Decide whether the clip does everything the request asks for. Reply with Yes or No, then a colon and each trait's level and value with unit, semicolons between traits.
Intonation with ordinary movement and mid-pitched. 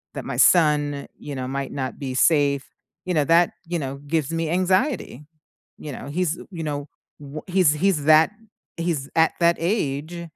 Yes: average, 3.3 semitones; medium, 155 Hz